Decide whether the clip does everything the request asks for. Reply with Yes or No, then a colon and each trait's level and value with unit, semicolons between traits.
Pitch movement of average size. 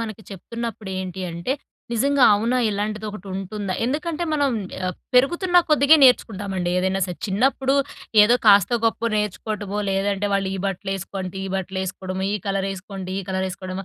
Yes: average, 3.6 semitones